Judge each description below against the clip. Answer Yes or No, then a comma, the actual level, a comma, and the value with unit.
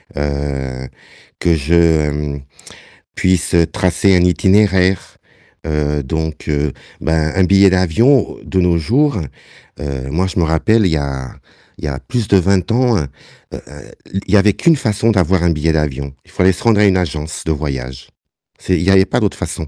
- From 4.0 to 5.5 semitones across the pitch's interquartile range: Yes, average, 4.6 semitones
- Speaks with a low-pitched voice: Yes, very low, 85 Hz